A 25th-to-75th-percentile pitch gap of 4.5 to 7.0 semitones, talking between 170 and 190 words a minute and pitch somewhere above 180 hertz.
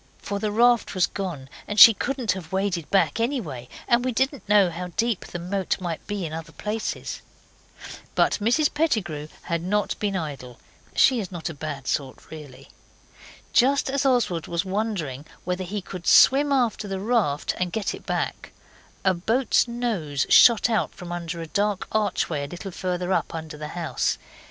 Yes: average, 5.2 semitones; average, 175 wpm; high, 190 Hz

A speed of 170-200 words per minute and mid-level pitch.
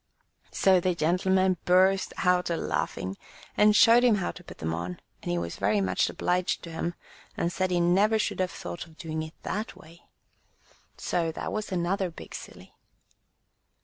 Yes: average, 180 wpm; medium, 180 Hz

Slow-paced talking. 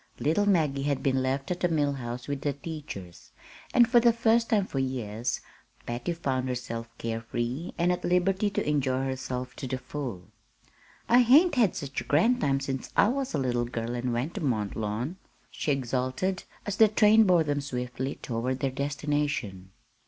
No: average, 185 wpm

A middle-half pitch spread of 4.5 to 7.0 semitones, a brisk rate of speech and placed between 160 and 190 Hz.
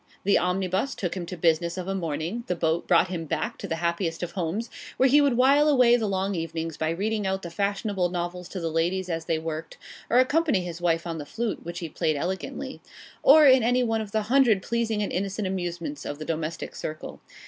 Yes: average, 4.8 semitones; fast, 225 wpm; medium, 185 Hz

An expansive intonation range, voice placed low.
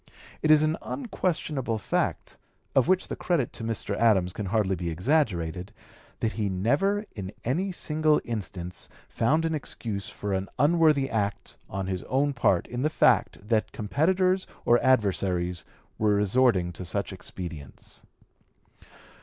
Yes: wide, 8.0 semitones; low, 115 Hz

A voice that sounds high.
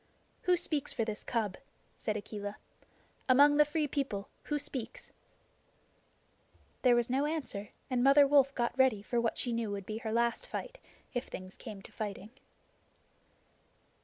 Yes: high, 240 Hz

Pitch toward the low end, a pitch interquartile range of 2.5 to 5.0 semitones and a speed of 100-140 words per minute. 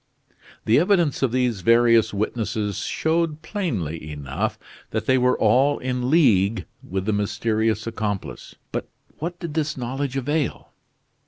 No: low, 120 Hz; wide, 5.5 semitones; slow, 135 wpm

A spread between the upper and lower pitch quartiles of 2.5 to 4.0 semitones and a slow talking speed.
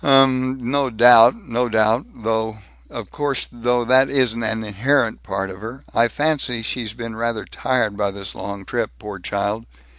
No: average, 3.0 semitones; average, 175 wpm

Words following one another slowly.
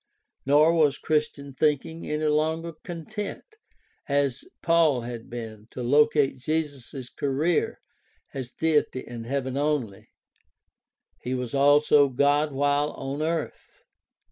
Yes: slow, 115 wpm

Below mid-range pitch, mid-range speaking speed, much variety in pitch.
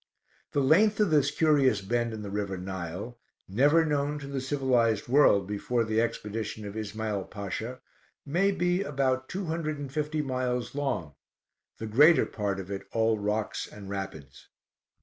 Yes: low, 120 Hz; average, 160 wpm; wide, 5.9 semitones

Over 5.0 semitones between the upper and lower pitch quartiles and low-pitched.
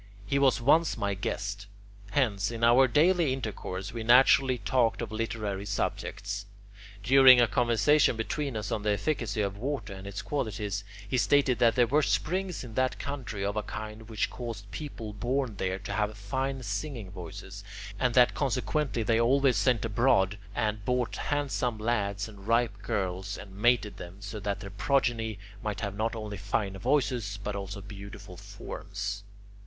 No: average, 4.0 semitones; low, 110 Hz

